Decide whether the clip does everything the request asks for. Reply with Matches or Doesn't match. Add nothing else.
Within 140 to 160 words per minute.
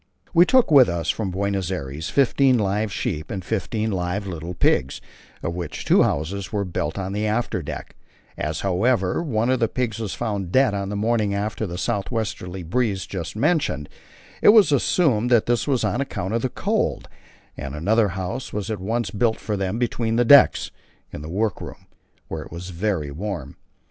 Doesn't match